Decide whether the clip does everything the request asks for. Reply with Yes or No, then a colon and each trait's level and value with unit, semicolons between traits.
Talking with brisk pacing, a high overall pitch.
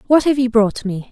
Yes: fast, 270 wpm; high, 235 Hz